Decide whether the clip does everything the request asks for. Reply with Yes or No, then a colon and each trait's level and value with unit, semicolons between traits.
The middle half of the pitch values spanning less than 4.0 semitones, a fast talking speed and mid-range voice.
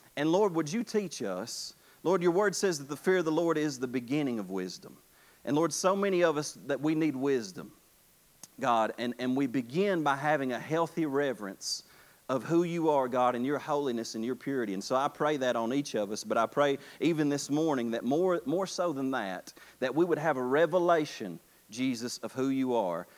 No: average, 4.6 semitones; fast, 215 wpm; medium, 145 Hz